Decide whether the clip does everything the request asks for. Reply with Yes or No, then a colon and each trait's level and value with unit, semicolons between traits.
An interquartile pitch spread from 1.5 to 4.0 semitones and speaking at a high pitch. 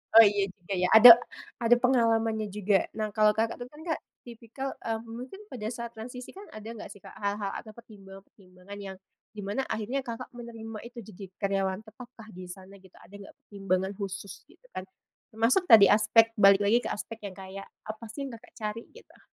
Yes: average, 2.9 semitones; high, 215 Hz